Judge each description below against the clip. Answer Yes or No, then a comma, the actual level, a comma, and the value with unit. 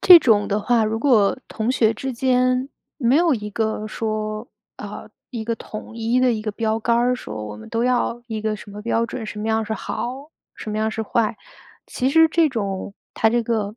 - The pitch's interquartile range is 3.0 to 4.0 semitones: No, narrow, 2.6 semitones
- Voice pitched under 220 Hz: No, high, 225 Hz